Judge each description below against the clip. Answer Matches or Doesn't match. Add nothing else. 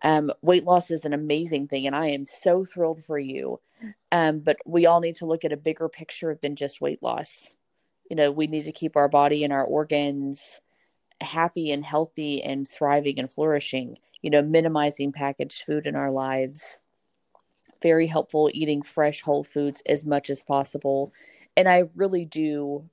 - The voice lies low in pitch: Doesn't match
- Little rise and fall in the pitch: Matches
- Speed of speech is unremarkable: Matches